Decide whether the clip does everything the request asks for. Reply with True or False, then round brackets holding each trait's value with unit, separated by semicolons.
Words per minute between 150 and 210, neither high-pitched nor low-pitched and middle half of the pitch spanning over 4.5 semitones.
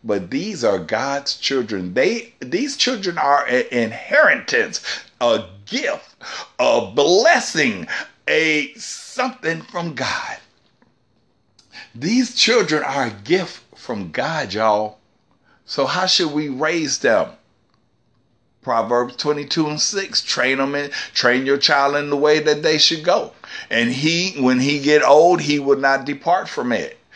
False (135 wpm; 145 Hz; 5.1 semitones)